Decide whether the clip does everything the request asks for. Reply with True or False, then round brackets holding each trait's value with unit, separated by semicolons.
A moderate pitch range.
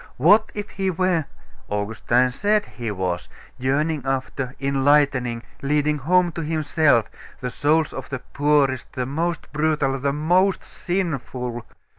True (4.1 semitones)